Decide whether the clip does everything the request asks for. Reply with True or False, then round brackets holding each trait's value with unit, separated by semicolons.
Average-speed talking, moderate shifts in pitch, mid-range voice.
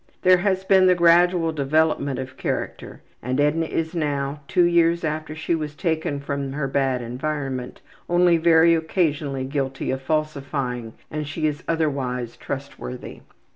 True (145 wpm; 3.4 semitones; 150 Hz)